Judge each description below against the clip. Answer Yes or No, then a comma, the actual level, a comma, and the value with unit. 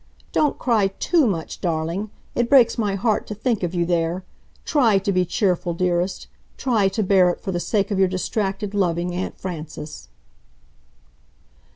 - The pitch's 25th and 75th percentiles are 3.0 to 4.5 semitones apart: Yes, average, 3.5 semitones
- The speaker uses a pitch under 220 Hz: Yes, high, 190 Hz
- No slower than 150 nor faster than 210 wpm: Yes, average, 165 wpm